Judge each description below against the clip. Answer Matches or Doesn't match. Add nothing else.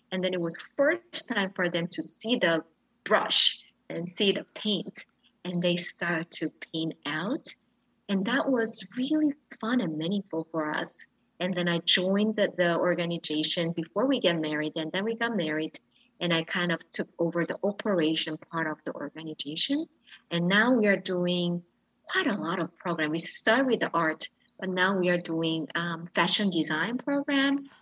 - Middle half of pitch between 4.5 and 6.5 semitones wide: Matches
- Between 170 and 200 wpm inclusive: Matches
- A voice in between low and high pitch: Matches